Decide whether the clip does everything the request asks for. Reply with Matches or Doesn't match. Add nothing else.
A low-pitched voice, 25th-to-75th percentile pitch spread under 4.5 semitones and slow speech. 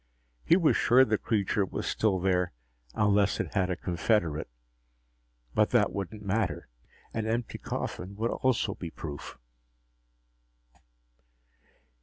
Matches